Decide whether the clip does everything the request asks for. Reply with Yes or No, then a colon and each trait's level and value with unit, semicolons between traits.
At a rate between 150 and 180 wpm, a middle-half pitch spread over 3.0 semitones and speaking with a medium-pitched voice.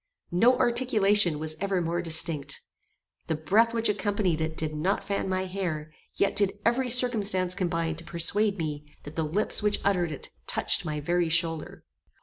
Yes: average, 165 wpm; average, 4.3 semitones; medium, 180 Hz